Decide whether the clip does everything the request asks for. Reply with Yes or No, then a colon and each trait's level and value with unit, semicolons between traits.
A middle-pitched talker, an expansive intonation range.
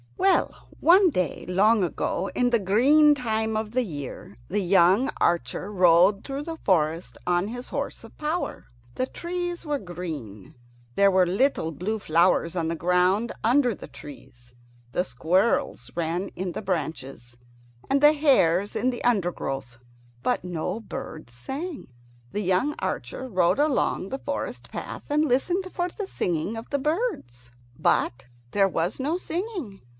No: high, 200 Hz; wide, 8.0 semitones